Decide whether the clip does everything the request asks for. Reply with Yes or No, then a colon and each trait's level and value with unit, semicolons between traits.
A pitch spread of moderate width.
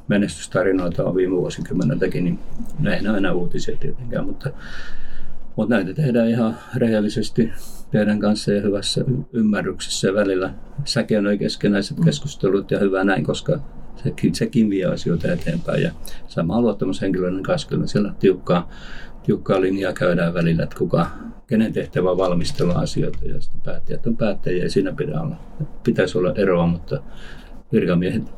Yes: average, 3.6 semitones